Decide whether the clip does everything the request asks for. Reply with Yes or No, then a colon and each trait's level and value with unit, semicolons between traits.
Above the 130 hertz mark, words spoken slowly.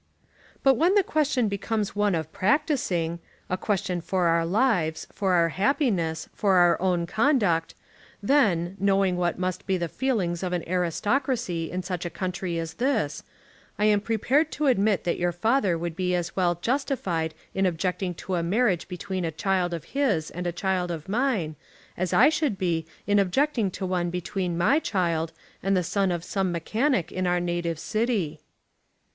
No: medium, 185 Hz; average, 175 wpm